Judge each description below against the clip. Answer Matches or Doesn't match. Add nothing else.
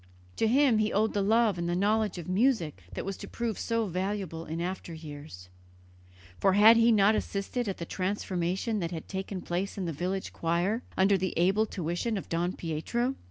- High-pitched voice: Matches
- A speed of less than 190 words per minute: Doesn't match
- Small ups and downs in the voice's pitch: Doesn't match